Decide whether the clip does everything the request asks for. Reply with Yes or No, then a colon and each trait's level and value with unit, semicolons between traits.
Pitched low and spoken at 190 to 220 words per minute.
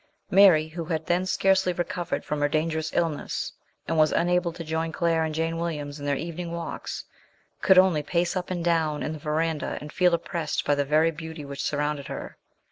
No: medium, 160 Hz; average, 200 wpm